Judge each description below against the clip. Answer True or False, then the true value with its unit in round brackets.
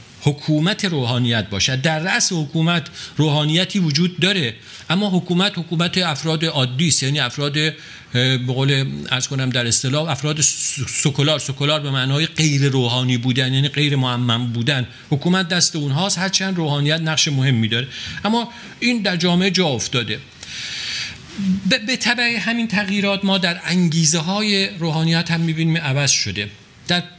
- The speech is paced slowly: False (150 wpm)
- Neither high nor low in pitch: True (155 Hz)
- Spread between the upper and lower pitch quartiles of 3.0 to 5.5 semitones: True (5.2 semitones)